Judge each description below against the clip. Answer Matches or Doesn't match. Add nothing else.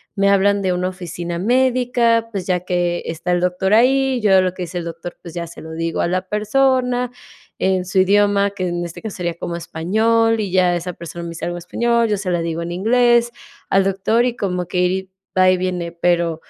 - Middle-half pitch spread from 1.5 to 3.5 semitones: Doesn't match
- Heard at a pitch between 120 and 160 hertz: Doesn't match